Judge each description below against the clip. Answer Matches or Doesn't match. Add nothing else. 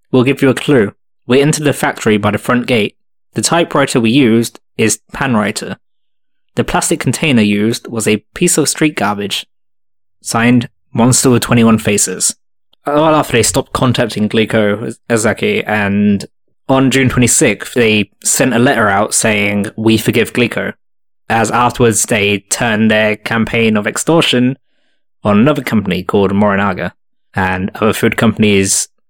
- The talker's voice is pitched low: Matches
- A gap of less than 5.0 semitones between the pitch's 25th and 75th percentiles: Matches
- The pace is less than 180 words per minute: Matches